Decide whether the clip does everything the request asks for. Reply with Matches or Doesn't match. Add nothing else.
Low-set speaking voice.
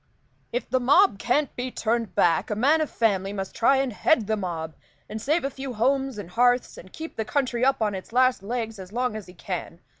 Doesn't match